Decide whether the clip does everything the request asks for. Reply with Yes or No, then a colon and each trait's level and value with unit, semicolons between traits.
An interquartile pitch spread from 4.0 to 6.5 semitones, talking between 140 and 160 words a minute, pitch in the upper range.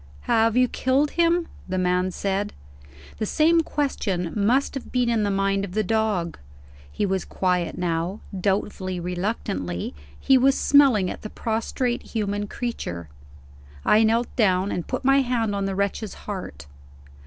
Yes: average, 4.7 semitones; average, 155 wpm; high, 205 Hz